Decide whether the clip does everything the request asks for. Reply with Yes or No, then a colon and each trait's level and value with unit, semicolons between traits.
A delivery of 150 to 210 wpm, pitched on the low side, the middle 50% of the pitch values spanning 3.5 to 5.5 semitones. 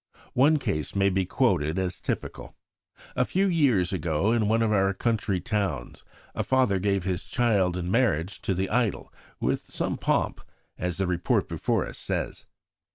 Yes: average, 165 wpm; very low, 95 Hz; average, 4.2 semitones